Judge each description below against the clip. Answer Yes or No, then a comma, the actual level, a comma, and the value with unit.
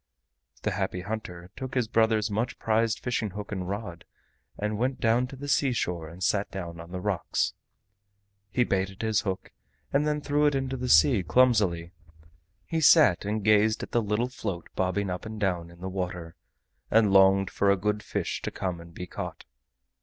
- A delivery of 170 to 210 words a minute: Yes, average, 185 wpm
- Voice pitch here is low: Yes, low, 105 Hz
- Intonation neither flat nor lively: Yes, average, 4.2 semitones